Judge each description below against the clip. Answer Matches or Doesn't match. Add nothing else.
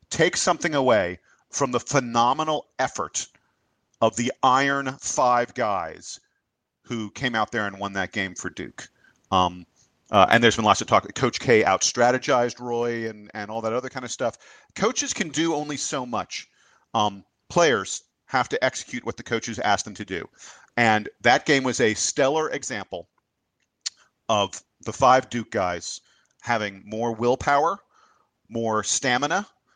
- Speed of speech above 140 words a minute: Matches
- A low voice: Matches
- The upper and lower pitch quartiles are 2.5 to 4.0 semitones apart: Matches